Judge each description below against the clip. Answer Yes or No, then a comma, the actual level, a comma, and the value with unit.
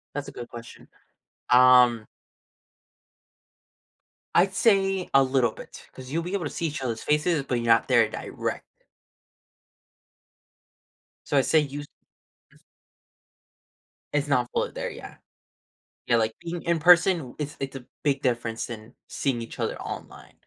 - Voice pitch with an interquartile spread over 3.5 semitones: Yes, average, 5.2 semitones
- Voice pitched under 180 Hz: Yes, low, 135 Hz